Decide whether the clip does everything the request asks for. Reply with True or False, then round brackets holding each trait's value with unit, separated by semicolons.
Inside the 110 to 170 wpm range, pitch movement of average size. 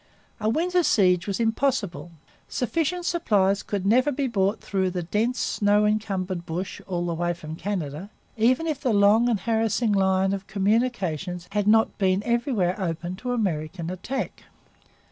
True (155 wpm; 4.2 semitones)